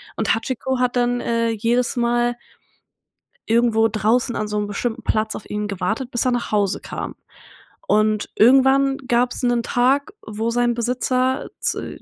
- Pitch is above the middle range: Yes, high, 240 Hz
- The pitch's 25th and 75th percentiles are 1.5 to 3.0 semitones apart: Yes, narrow, 2.4 semitones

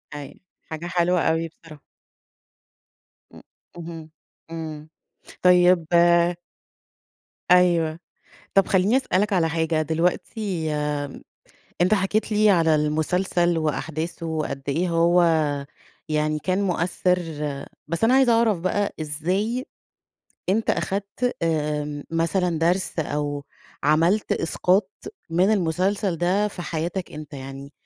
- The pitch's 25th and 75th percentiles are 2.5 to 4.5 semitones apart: Yes, average, 3.2 semitones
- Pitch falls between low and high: Yes, medium, 170 Hz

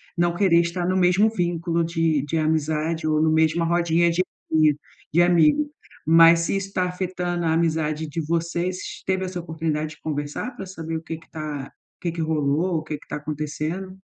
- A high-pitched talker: No, medium, 165 Hz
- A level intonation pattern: Yes, narrow, 2.1 semitones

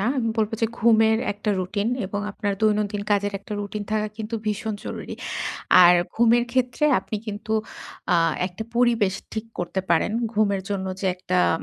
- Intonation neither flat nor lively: No, narrow, 1.8 semitones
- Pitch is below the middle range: No, high, 210 Hz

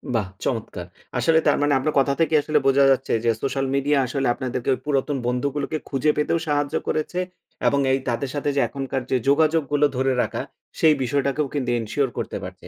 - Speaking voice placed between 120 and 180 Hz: Yes, medium, 140 Hz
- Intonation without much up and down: Yes, narrow, 2.0 semitones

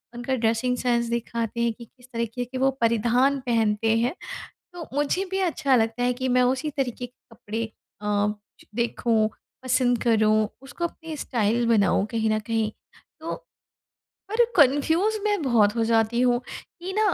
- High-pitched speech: Yes, high, 240 Hz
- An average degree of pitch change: Yes, average, 3.2 semitones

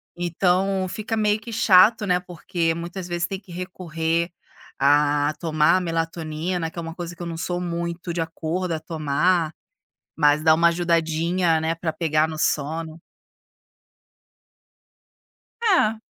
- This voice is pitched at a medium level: Yes, medium, 170 Hz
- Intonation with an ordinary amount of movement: No, narrow, 2.1 semitones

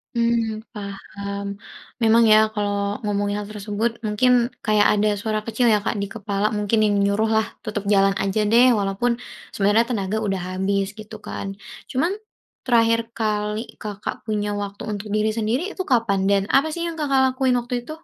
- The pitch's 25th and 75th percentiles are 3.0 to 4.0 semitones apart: No, narrow, 2.4 semitones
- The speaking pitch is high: Yes, high, 215 Hz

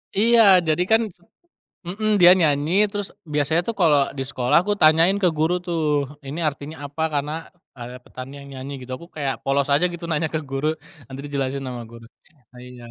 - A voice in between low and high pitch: Yes, medium, 150 Hz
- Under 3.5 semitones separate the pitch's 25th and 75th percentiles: No, average, 4.3 semitones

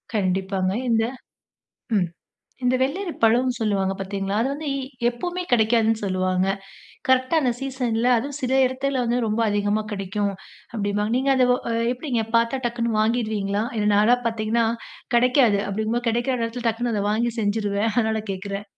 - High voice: Yes, high, 225 Hz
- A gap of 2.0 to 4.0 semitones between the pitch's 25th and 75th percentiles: Yes, average, 3.3 semitones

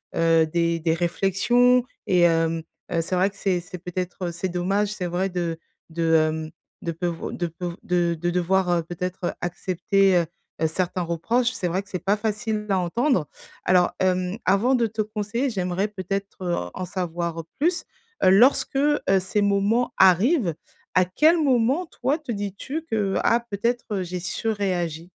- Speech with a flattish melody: No, average, 3.6 semitones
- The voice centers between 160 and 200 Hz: Yes, medium, 185 Hz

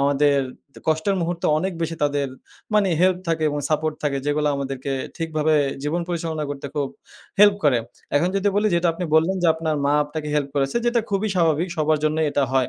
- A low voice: No, medium, 155 Hz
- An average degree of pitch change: Yes, average, 3.0 semitones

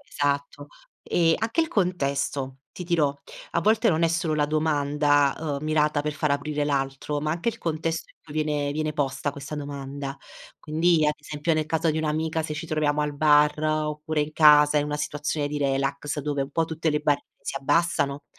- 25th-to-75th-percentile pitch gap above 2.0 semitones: No, narrow, 1.6 semitones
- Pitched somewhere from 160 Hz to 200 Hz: No, medium, 150 Hz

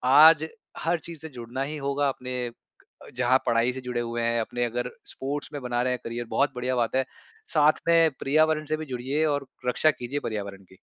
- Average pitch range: Yes, average, 3.6 semitones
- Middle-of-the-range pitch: No, low, 130 Hz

